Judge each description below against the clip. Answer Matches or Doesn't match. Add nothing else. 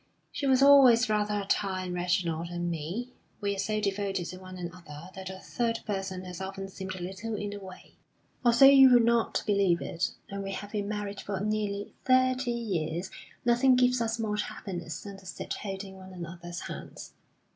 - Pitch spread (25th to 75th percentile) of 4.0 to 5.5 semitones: Doesn't match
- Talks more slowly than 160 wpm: Doesn't match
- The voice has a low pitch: Doesn't match